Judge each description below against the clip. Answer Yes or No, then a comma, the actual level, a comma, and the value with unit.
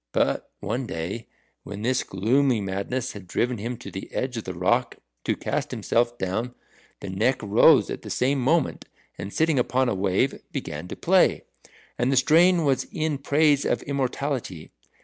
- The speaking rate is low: No, average, 170 wpm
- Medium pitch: No, low, 125 Hz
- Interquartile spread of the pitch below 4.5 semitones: No, average, 5.3 semitones